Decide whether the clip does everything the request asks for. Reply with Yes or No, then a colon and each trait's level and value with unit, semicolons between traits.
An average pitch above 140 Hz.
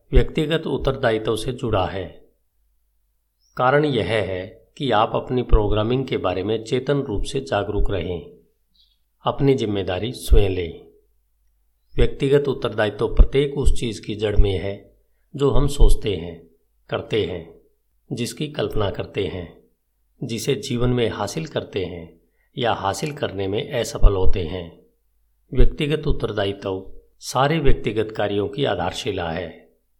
No: low, 110 Hz